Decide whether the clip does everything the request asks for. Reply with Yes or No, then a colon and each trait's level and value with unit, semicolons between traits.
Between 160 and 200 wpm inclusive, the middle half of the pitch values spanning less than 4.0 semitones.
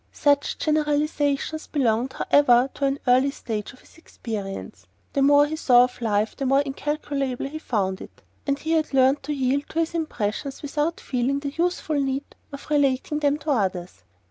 Yes: average, 175 wpm; average, 3.1 semitones